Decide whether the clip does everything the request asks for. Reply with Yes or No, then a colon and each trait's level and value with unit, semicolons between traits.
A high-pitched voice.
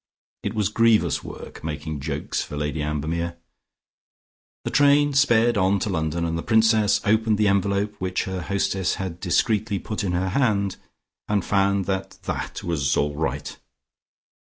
No: very low, 95 Hz